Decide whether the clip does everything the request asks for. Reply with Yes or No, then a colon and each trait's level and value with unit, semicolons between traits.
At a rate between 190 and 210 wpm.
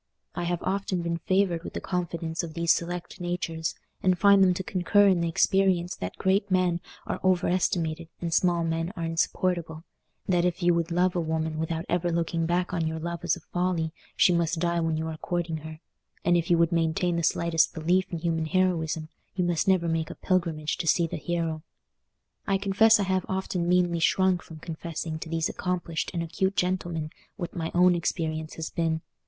Yes: average, 200 wpm